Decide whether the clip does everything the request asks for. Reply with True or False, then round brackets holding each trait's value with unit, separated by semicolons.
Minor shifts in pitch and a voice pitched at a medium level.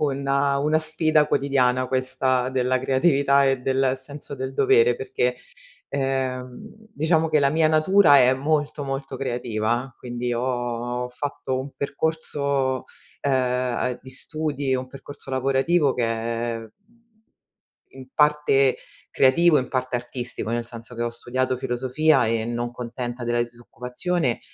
False (2.3 semitones; 130 Hz)